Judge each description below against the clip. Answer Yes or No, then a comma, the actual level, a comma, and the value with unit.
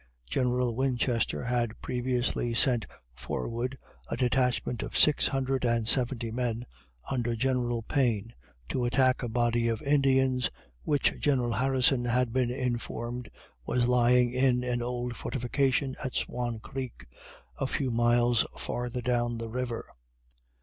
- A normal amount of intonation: No, narrow, 1.4 semitones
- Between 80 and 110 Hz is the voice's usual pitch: No, low, 125 Hz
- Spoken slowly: Yes, slow, 130 wpm